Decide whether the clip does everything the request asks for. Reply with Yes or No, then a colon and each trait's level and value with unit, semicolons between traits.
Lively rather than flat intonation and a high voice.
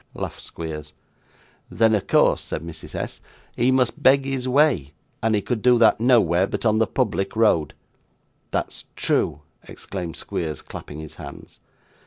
No: wide, 7.1 semitones; low, 110 Hz